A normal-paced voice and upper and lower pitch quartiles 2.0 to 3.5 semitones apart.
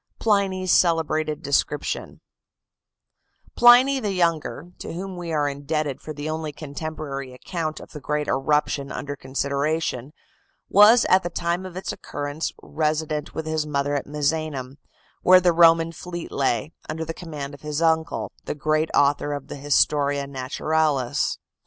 Yes: average, 145 wpm; average, 2.7 semitones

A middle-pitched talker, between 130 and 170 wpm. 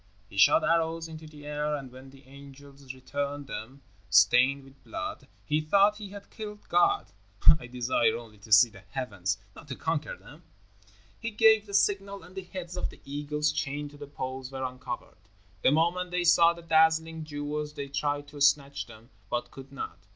No: medium, 145 Hz; average, 190 wpm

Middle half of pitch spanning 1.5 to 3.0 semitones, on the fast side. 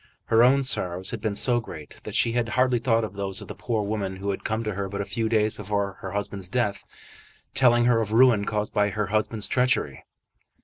Yes: average, 2.7 semitones; fast, 225 wpm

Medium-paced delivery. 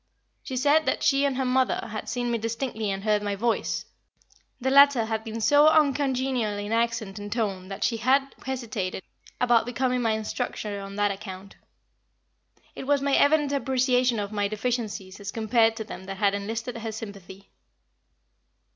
Yes: average, 170 wpm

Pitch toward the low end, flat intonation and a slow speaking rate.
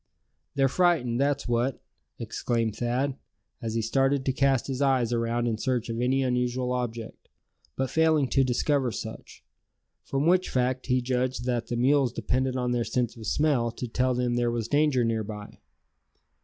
No: low, 125 Hz; narrow, 2.2 semitones; average, 170 wpm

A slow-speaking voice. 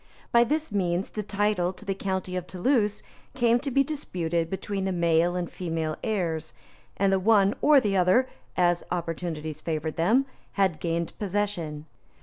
No: average, 160 wpm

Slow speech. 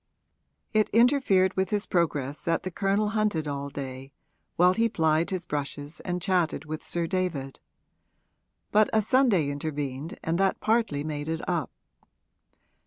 No: average, 145 wpm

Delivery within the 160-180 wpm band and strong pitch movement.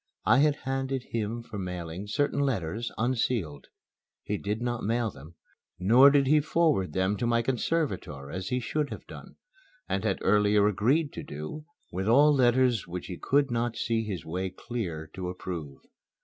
Yes: average, 170 wpm; wide, 5.9 semitones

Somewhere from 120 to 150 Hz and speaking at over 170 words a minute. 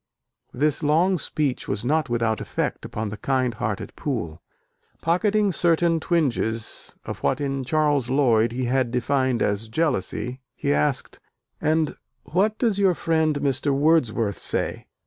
No: low, 135 Hz; average, 140 wpm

